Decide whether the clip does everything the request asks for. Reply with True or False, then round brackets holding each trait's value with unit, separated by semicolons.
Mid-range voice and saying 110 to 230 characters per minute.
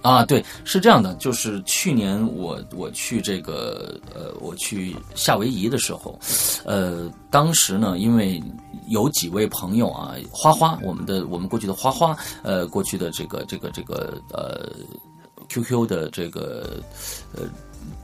False (115 Hz; 215 characters per minute)